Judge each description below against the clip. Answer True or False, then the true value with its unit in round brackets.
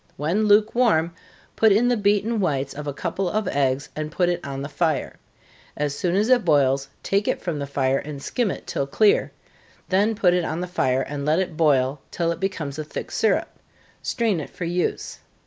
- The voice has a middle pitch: True (170 Hz)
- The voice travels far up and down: True (6.0 semitones)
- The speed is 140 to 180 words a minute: False (205 wpm)